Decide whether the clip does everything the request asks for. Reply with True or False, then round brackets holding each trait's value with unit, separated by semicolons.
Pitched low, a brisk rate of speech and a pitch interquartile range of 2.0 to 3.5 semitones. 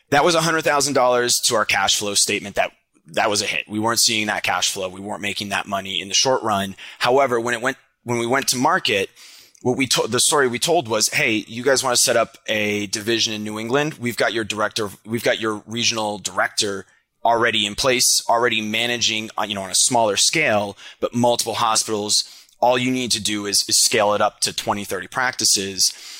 True (115 Hz; 220 wpm; 3.0 semitones)